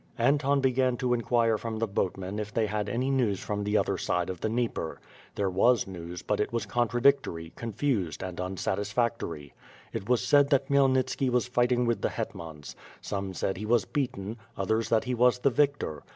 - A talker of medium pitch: No, low, 115 Hz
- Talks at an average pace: Yes, average, 185 wpm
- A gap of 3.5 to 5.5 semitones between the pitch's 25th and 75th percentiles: Yes, average, 4.4 semitones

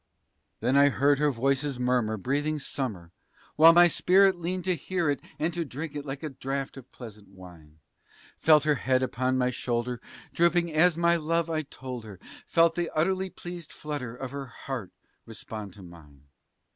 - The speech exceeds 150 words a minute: Yes, average, 175 wpm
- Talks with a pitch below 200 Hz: Yes, medium, 140 Hz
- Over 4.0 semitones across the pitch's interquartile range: Yes, average, 5.2 semitones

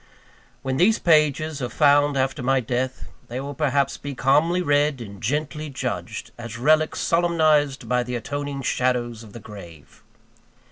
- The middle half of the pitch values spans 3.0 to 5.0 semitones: Yes, average, 3.5 semitones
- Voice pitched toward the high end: No, medium, 140 Hz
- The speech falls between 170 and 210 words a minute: No, average, 150 wpm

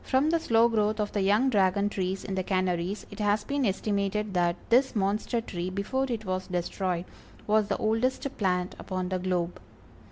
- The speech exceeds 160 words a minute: Yes, average, 185 wpm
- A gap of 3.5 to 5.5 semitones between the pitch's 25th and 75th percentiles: No, average, 3.0 semitones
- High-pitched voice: Yes, high, 200 Hz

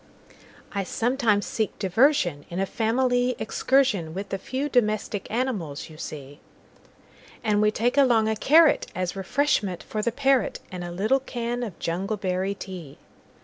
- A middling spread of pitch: Yes, average, 5.0 semitones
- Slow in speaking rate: Yes, slow, 125 wpm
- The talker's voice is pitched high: Yes, high, 215 Hz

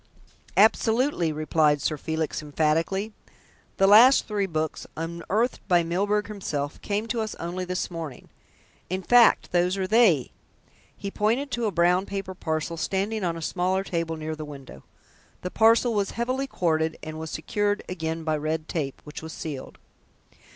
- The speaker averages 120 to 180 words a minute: Yes, average, 160 wpm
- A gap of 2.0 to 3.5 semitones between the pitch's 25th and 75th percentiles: No, average, 4.7 semitones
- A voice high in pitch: No, medium, 180 Hz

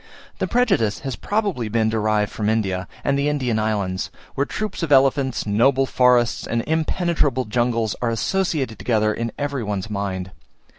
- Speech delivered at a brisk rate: No, average, 155 wpm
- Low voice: Yes, low, 120 Hz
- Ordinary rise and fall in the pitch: Yes, average, 4.5 semitones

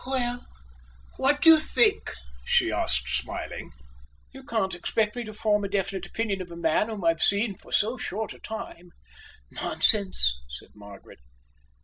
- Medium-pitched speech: No, high, 205 Hz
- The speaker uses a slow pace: No, average, 155 wpm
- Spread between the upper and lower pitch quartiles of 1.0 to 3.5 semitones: No, average, 5.1 semitones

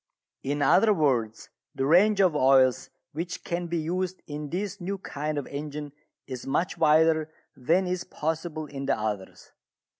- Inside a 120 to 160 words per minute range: Yes, average, 155 wpm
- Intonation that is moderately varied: Yes, average, 4.1 semitones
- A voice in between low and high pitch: Yes, medium, 155 Hz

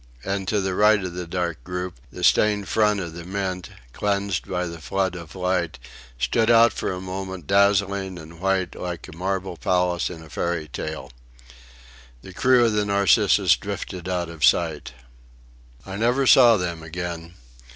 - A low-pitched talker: Yes, very low, 90 Hz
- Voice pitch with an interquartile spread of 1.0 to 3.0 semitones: Yes, narrow, 2.6 semitones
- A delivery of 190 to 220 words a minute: No, average, 170 wpm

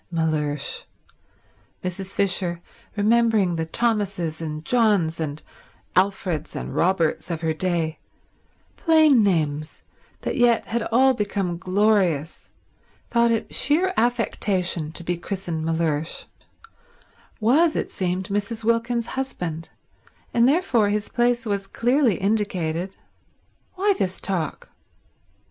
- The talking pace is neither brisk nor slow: No, slow, 105 wpm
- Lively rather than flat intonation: Yes, wide, 5.9 semitones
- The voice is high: Yes, high, 195 Hz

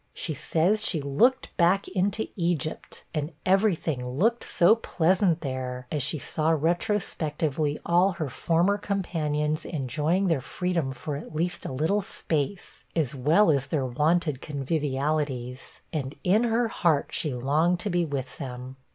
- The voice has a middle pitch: Yes, medium, 160 Hz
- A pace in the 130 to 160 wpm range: Yes, average, 150 wpm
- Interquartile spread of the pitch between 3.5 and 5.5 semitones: Yes, average, 4.3 semitones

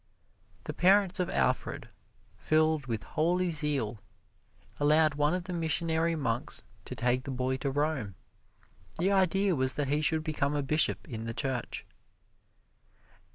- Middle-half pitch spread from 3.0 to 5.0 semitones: Yes, average, 4.1 semitones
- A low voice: No, medium, 150 Hz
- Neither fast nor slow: Yes, average, 145 wpm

